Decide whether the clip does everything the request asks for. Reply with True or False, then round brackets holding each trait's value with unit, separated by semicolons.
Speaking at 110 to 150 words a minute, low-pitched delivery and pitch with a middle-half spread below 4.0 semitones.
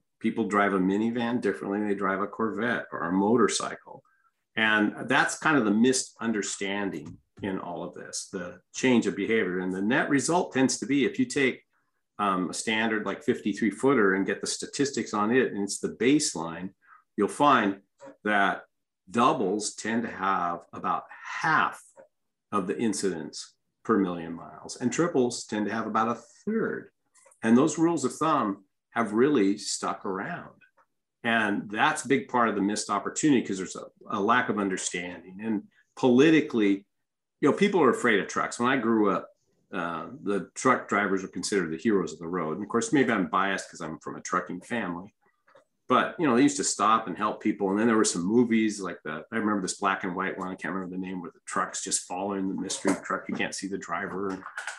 False (200 wpm; 105 Hz; 3.4 semitones)